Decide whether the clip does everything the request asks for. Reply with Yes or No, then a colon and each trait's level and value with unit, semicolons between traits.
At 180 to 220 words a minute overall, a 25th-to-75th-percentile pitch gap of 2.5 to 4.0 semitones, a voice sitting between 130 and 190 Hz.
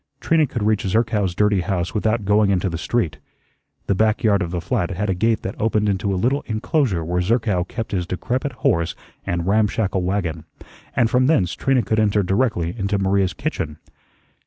No: average, 185 wpm; average, 3.7 semitones; low, 100 Hz